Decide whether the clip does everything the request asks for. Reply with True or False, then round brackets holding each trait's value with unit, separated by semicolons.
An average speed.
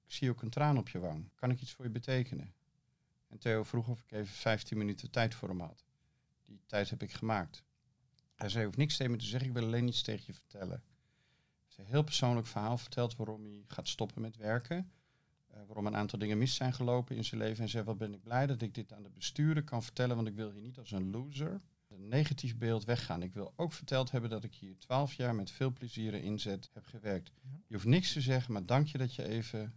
False (255 wpm)